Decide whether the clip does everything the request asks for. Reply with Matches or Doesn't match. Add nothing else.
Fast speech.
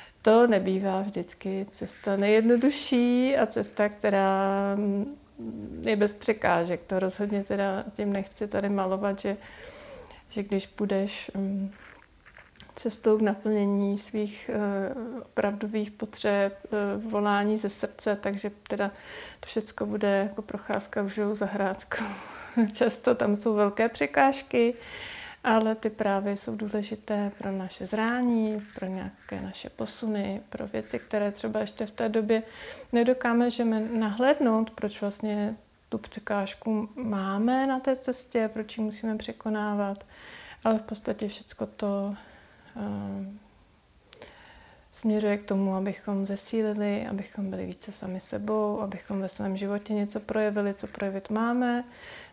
Doesn't match